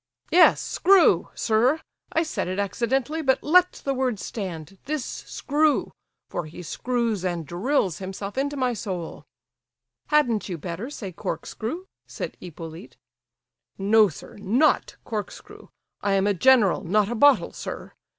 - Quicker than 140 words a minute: No, slow, 135 wpm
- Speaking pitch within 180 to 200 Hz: No, high, 220 Hz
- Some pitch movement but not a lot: No, wide, 6.4 semitones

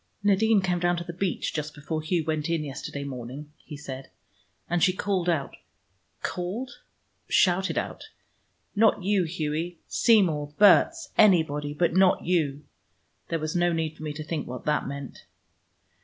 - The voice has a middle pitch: Yes, medium, 165 Hz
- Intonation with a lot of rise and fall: No, average, 3.7 semitones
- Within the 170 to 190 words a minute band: No, average, 155 wpm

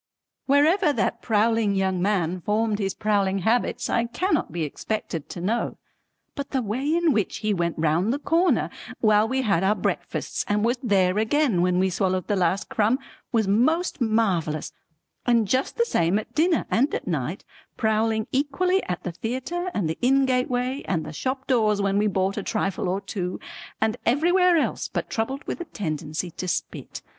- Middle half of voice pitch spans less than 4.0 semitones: No, wide, 5.5 semitones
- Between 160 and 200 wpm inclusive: Yes, average, 180 wpm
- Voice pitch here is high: Yes, high, 215 Hz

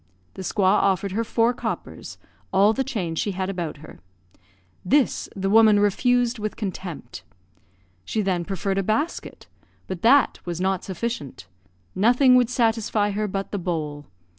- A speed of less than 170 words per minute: Yes, average, 150 wpm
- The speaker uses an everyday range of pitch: Yes, average, 3.6 semitones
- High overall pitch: Yes, high, 200 Hz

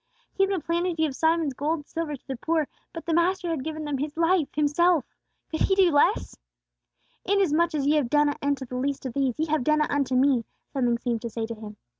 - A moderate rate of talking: No, fast, 245 wpm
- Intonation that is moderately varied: Yes, average, 3.8 semitones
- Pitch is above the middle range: Yes, very high, 295 Hz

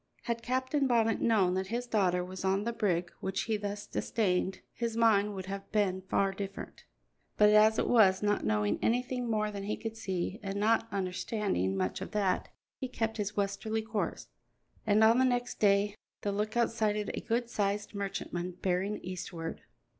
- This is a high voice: Yes, high, 205 Hz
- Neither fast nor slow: Yes, average, 175 wpm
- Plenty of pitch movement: No, average, 2.8 semitones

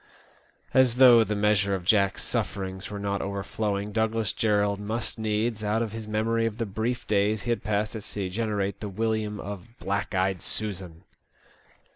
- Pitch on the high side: No, low, 105 Hz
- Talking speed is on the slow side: No, average, 175 wpm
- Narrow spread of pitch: Yes, narrow, 1.9 semitones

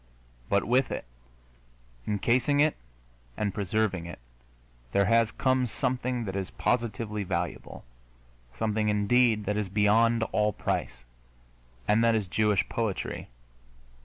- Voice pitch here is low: Yes, low, 105 Hz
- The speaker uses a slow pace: Yes, slow, 120 wpm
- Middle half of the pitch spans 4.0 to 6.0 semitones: No, narrow, 2.6 semitones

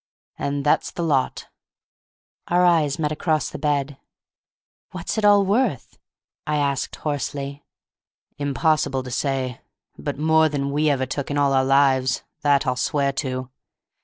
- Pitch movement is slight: Yes, narrow, 2.3 semitones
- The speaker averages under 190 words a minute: Yes, average, 150 wpm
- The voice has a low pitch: No, medium, 145 Hz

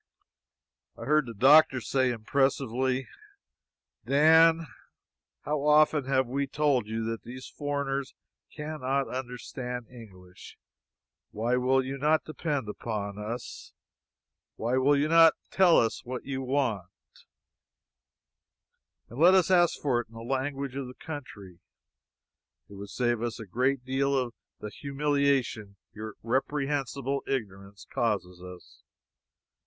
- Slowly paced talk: Yes, slow, 125 wpm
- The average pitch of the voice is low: Yes, low, 130 Hz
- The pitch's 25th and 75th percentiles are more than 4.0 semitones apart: No, average, 3.7 semitones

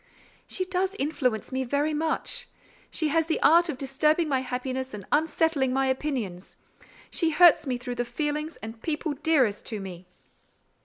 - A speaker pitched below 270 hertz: No, very high, 280 Hz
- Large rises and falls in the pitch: No, average, 4.2 semitones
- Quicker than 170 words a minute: No, average, 160 wpm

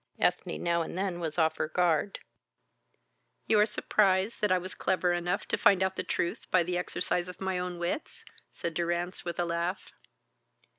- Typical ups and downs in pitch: No, narrow, 1.6 semitones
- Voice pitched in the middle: Yes, medium, 180 Hz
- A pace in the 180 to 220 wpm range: Yes, average, 185 wpm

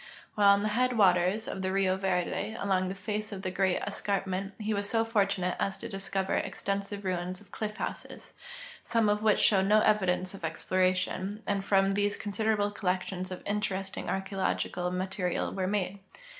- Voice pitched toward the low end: No, high, 195 Hz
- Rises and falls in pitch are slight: Yes, narrow, 1.9 semitones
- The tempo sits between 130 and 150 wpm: No, average, 175 wpm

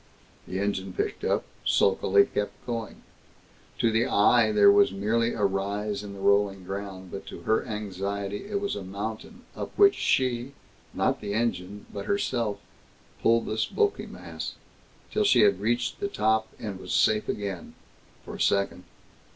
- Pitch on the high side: No, low, 105 Hz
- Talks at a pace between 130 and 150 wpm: No, average, 160 wpm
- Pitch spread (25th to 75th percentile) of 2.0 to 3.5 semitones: Yes, average, 2.8 semitones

